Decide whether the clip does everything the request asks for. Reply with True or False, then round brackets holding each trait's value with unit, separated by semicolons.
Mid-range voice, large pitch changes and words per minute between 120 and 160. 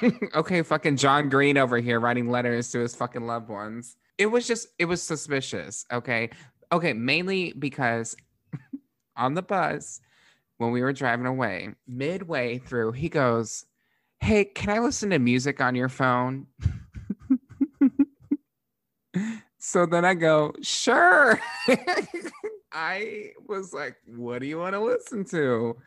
True (145 Hz; 8.8 semitones; 135 wpm)